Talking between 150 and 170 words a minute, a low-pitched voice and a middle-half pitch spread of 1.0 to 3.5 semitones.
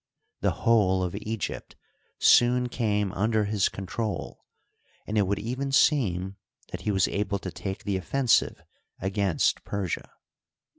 No: slow, 135 wpm; low, 105 Hz; average, 3.1 semitones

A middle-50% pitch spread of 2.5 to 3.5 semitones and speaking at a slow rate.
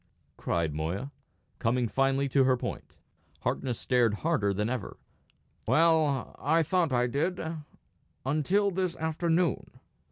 No: average, 5.1 semitones; slow, 120 wpm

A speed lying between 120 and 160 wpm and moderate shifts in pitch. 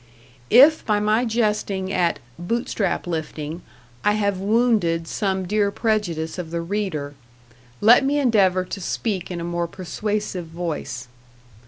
Yes: slow, 135 wpm; average, 3.9 semitones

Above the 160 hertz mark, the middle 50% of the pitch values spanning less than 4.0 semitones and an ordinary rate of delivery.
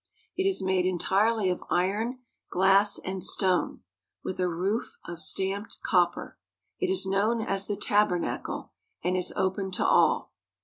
Yes: high, 190 Hz; narrow, 2.4 semitones; average, 145 wpm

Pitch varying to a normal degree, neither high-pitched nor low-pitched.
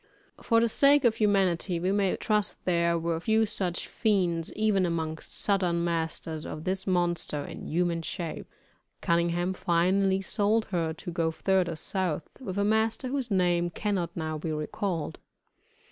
Yes: average, 3.2 semitones; medium, 180 Hz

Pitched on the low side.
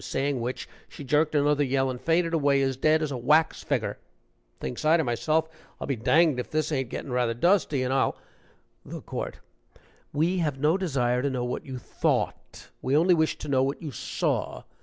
No: medium, 145 Hz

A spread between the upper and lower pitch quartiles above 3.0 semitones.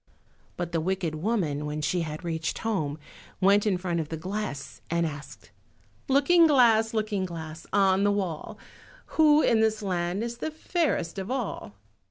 Yes: wide, 5.4 semitones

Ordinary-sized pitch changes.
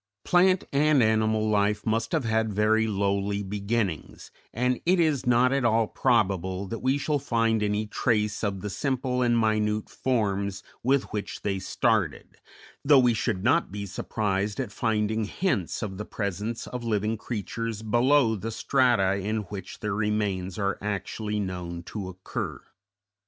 Yes: average, 3.0 semitones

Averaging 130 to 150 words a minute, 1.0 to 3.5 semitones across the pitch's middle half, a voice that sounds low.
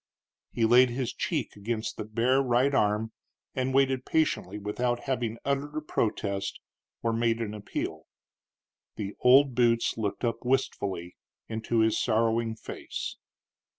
Yes: slow, 135 wpm; average, 2.9 semitones; low, 115 Hz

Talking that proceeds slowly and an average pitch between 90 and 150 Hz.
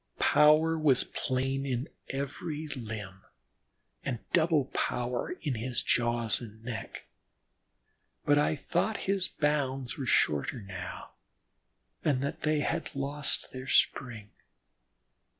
Yes: slow, 115 wpm; low, 135 Hz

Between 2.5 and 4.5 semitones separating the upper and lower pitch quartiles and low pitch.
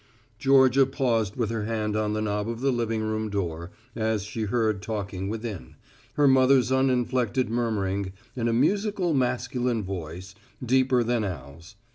Yes: average, 3.7 semitones; low, 115 Hz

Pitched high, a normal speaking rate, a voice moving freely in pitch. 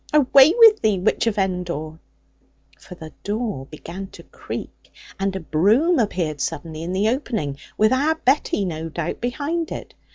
Yes: high, 195 Hz; average, 160 wpm; wide, 7.9 semitones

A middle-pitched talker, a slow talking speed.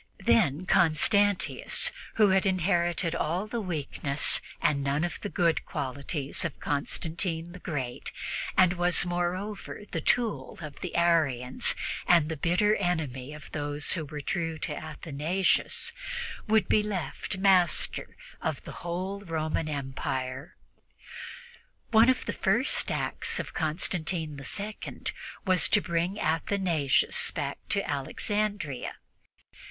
Yes: medium, 170 Hz; slow, 125 wpm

